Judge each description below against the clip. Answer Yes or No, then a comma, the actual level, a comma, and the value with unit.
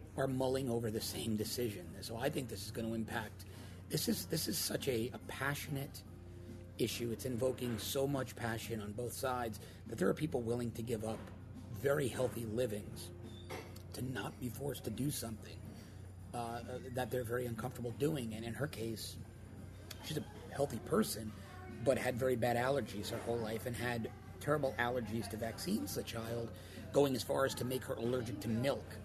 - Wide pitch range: No, average, 3.3 semitones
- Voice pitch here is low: Yes, low, 115 Hz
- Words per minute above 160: Yes, average, 185 wpm